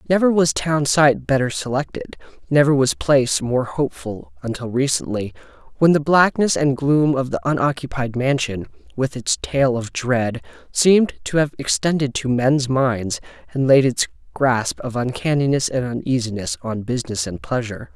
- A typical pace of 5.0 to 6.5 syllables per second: No, 4.8 syllables/s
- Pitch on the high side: No, low, 130 Hz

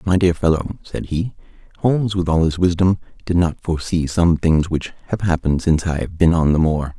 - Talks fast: Yes, fast, 215 wpm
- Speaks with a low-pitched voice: Yes, very low, 85 Hz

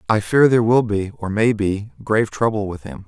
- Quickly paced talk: Yes, fast, 235 wpm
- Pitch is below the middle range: Yes, low, 105 Hz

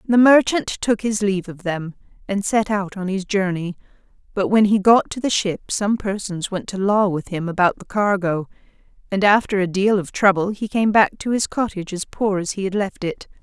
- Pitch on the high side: Yes, high, 200 Hz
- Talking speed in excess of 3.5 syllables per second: Yes, 5.1 syllables/s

